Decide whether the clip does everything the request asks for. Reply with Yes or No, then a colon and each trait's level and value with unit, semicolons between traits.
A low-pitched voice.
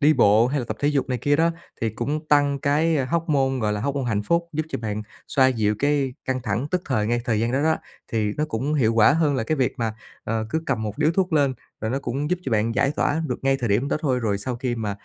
Yes: low, 130 Hz